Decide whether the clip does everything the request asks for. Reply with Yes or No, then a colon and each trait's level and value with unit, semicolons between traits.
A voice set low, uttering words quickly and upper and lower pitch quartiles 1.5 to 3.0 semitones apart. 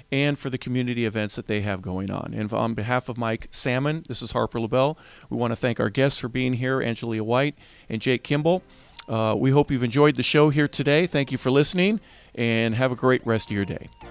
No: low, 125 Hz; fast, 235 wpm; average, 3.7 semitones